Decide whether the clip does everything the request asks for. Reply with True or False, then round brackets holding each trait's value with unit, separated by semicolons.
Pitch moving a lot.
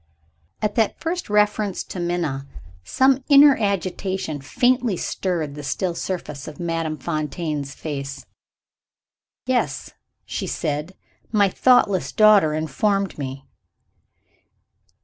True (5.7 semitones)